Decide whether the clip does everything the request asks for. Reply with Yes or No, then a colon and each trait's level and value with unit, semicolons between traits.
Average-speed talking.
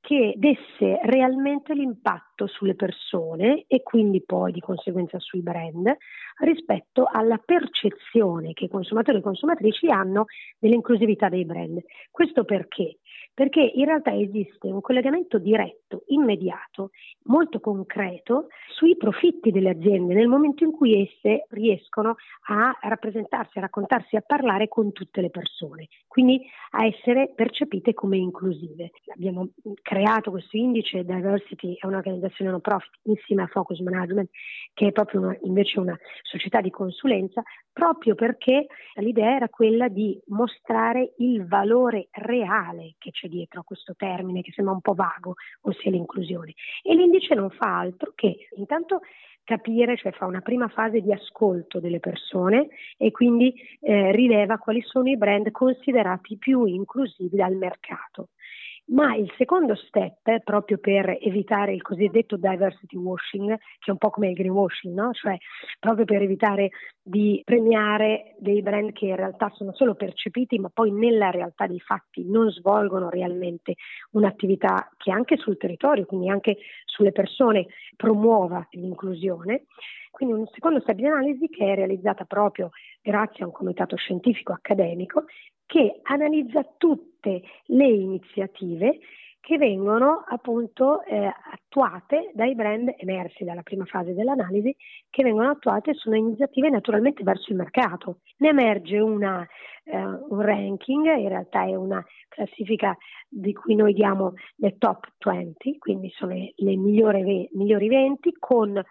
Yes: average, 145 wpm